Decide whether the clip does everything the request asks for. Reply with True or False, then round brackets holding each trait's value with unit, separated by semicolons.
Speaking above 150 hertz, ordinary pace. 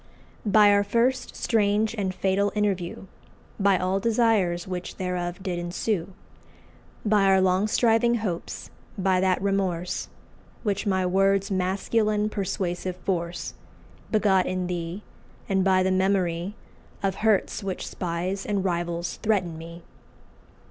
False (190 Hz; 125 wpm)